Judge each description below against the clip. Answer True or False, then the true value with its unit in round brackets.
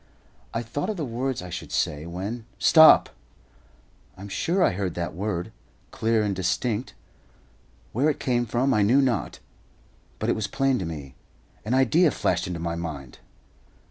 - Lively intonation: True (6.6 semitones)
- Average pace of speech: True (170 wpm)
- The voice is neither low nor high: False (110 Hz)